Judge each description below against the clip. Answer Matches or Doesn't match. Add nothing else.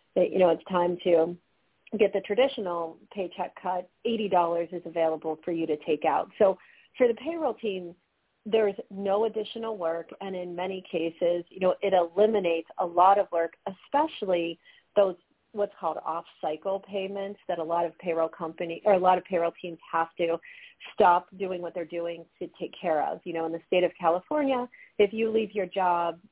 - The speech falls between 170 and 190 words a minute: Matches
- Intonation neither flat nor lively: Matches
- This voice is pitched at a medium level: Matches